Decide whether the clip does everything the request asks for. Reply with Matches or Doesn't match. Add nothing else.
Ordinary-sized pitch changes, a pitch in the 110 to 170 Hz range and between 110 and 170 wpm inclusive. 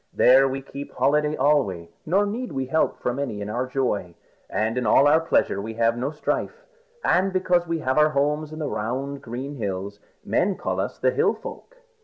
Doesn't match